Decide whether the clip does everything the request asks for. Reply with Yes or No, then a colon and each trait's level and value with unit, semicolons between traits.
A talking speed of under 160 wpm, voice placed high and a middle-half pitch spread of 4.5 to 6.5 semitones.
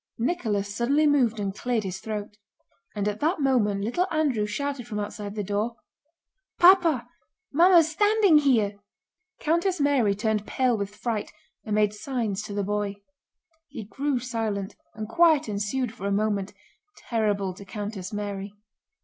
Yes: average, 150 wpm; high, 220 Hz; wide, 5.4 semitones